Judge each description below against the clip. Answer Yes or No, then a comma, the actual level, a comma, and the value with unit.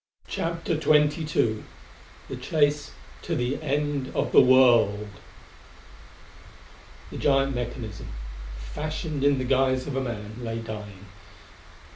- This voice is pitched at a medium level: No, low, 130 Hz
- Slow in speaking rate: Yes, slow, 110 wpm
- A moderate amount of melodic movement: Yes, average, 4.4 semitones